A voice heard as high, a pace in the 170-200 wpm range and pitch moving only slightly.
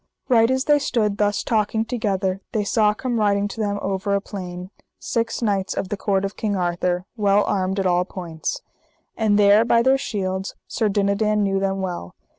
Yes: high, 200 Hz; average, 190 wpm; narrow, 2.2 semitones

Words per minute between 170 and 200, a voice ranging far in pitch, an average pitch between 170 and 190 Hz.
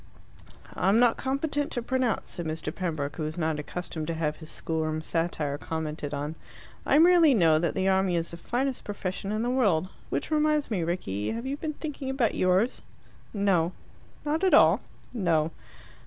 Yes: average, 180 wpm; wide, 8.2 semitones; medium, 185 Hz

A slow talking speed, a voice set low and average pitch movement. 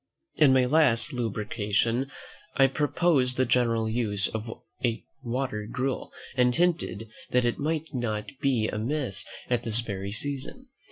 Yes: slow, 130 wpm; low, 125 Hz; average, 3.5 semitones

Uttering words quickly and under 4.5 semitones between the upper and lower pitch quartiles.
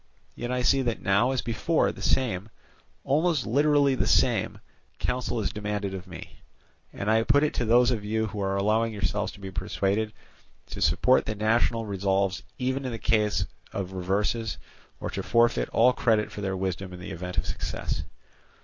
No: average, 185 wpm; average, 3.8 semitones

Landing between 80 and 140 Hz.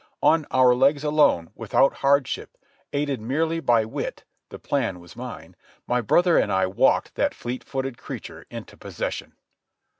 Yes: low, 135 Hz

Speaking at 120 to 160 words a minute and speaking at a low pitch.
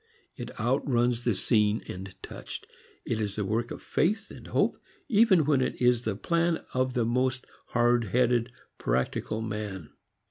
Yes: average, 155 wpm; low, 120 Hz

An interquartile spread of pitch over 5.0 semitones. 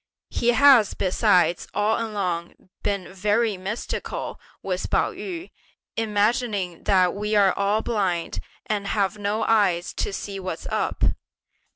No: average, 2.7 semitones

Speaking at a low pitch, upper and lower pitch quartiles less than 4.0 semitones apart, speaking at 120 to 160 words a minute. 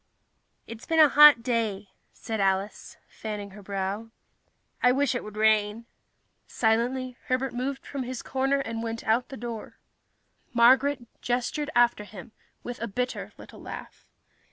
No: high, 235 Hz; average, 3.1 semitones; average, 145 wpm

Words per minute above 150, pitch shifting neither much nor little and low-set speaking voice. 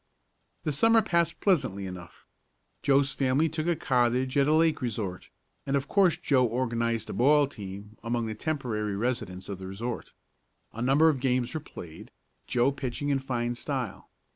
Yes: average, 165 wpm; average, 4.1 semitones; low, 130 Hz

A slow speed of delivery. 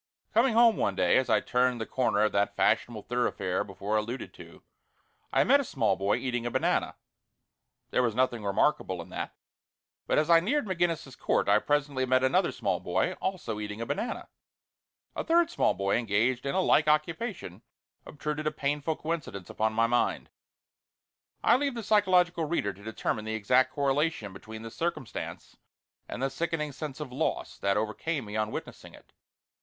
No: average, 175 wpm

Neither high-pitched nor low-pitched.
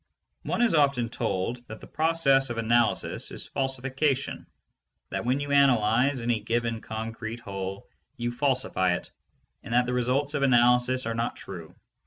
No: low, 125 Hz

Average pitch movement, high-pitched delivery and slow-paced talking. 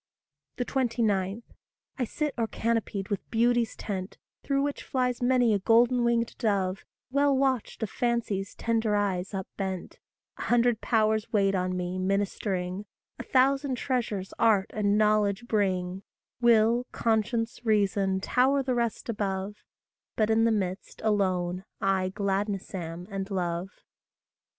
Yes: average, 3.6 semitones; high, 215 Hz; slow, 130 wpm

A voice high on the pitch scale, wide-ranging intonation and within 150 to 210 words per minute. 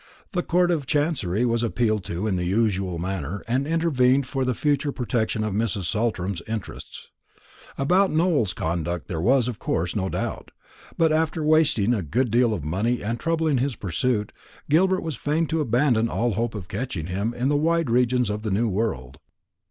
No: low, 120 Hz; wide, 6.5 semitones; average, 185 wpm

